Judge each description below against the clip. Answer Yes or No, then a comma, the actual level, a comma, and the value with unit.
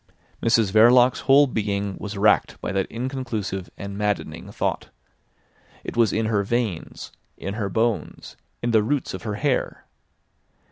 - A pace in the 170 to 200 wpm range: No, average, 145 wpm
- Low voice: Yes, low, 110 Hz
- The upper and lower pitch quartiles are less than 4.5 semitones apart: Yes, average, 3.1 semitones